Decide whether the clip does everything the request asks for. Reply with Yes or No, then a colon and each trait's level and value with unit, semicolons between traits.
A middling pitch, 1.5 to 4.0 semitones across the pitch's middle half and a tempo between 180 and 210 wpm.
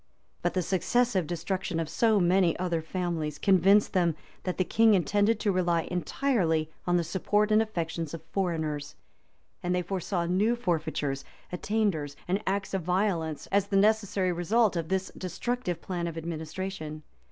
No: medium, 180 Hz; average, 3.3 semitones; average, 155 wpm